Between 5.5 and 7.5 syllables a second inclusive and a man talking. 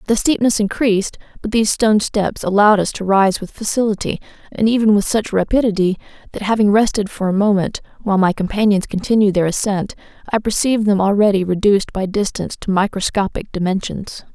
No: 6.0 syllables/s; female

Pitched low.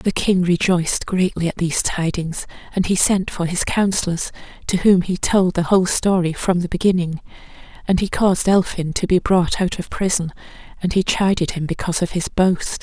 No: medium, 180 Hz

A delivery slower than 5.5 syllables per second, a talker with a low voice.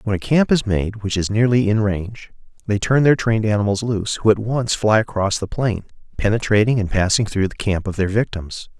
No: 5.6 syllables/s; low, 105 Hz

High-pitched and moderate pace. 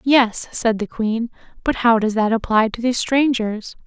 Yes: high, 230 Hz; average, 185 wpm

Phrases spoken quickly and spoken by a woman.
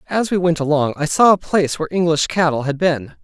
No: fast, 240 wpm; male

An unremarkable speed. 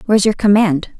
Yes: average, 180 wpm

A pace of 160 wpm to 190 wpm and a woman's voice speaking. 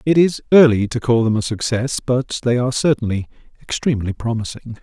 No: average, 175 wpm; male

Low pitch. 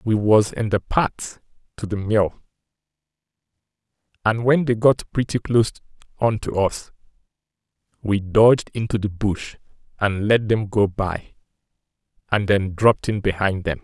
Yes: low, 105 Hz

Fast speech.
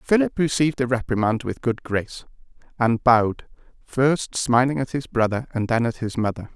No: average, 175 wpm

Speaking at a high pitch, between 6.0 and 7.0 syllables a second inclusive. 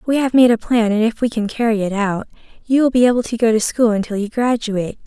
Yes: high, 225 Hz; 6.2 syllables/s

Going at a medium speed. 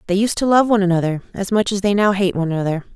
No: fast, 285 wpm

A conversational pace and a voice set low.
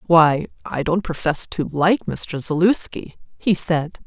No: average, 150 wpm; medium, 165 Hz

